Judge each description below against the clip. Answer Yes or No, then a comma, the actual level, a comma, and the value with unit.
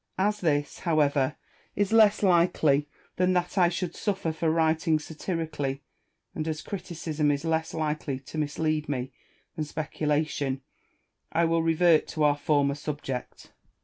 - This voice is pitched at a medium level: Yes, medium, 155 Hz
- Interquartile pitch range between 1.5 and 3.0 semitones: Yes, narrow, 2.5 semitones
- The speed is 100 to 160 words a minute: Yes, average, 140 wpm